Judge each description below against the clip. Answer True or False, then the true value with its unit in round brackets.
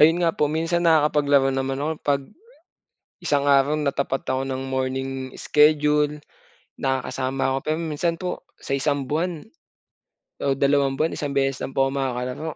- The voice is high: False (140 Hz)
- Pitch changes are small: True (2.1 semitones)